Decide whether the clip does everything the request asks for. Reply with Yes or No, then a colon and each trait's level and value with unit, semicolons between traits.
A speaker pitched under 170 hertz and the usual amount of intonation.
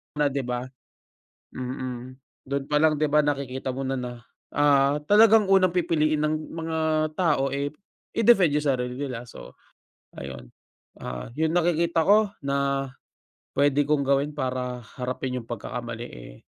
Yes: medium, 140 Hz; average, 3.4 semitones